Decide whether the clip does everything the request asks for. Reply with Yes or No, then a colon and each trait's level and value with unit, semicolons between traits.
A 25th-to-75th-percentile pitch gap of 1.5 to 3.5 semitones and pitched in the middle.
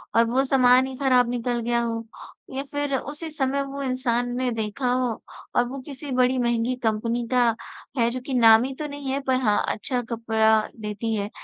No: narrow, 2.5 semitones; very high, 250 Hz